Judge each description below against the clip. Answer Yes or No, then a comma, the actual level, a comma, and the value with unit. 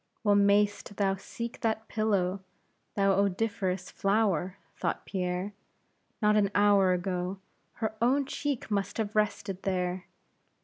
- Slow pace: Yes, slow, 125 wpm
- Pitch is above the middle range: Yes, high, 200 Hz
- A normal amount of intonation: No, narrow, 2.2 semitones